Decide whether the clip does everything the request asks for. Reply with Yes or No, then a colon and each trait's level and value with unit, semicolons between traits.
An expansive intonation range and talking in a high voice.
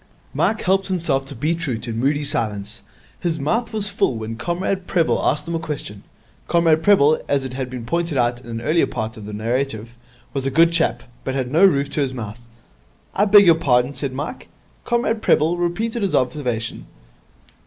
No: wide, 5.9 semitones; medium, 140 Hz